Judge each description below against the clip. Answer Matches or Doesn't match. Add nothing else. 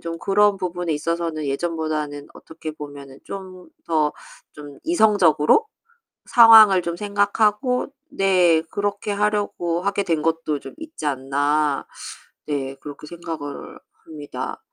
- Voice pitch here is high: Doesn't match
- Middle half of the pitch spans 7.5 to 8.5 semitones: Doesn't match